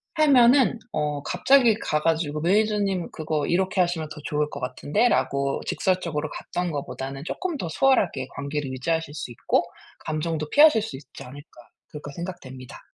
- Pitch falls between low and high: Yes, medium, 160 Hz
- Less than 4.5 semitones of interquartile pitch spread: No, average, 5.3 semitones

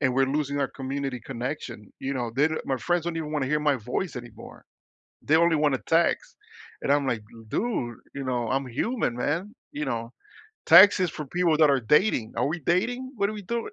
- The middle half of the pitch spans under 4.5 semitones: No, average, 4.9 semitones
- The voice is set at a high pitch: No, medium, 145 Hz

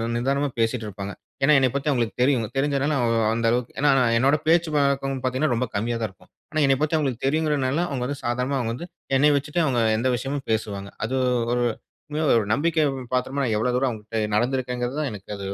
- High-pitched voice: No, low, 130 Hz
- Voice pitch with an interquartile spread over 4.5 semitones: No, average, 3.5 semitones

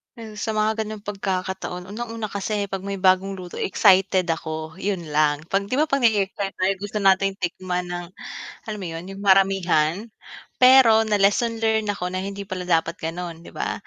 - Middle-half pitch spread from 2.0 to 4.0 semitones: Yes, average, 2.7 semitones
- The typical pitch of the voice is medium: No, high, 195 Hz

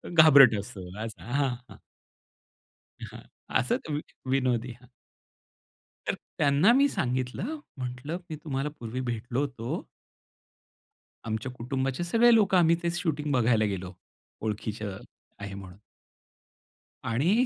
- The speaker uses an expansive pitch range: Yes, wide, 5.7 semitones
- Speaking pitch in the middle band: No, low, 130 Hz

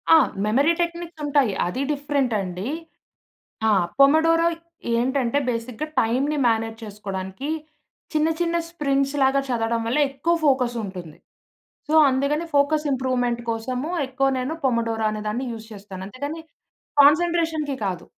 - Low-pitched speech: No, very high, 265 Hz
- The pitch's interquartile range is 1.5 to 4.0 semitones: No, average, 4.8 semitones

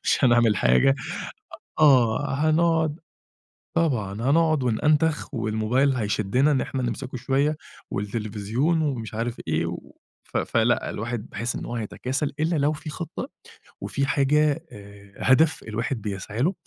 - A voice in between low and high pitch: No, low, 130 Hz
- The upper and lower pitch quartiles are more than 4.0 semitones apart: Yes, wide, 5.4 semitones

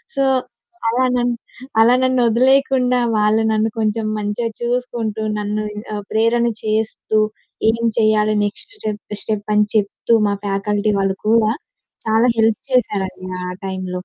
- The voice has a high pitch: Yes, high, 220 Hz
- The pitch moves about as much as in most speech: No, narrow, 2.2 semitones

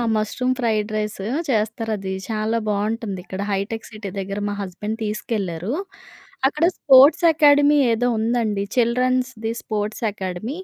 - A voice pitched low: No, high, 220 Hz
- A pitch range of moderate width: Yes, average, 3.2 semitones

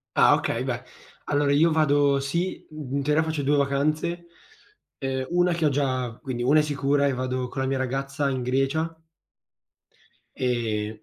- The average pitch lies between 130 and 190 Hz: Yes, medium, 140 Hz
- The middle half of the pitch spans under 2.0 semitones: No, average, 2.7 semitones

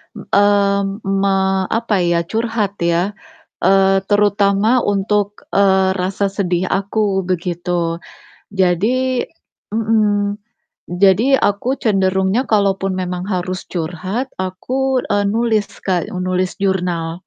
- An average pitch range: No, narrow, 2.1 semitones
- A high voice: Yes, high, 195 Hz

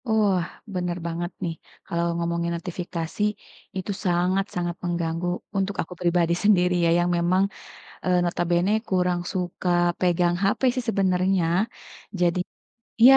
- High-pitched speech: No, medium, 180 Hz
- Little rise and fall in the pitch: Yes, narrow, 1.5 semitones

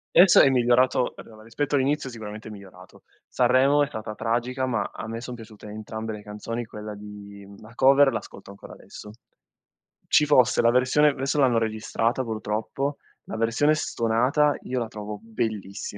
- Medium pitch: No, low, 115 Hz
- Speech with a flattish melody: No, average, 3.5 semitones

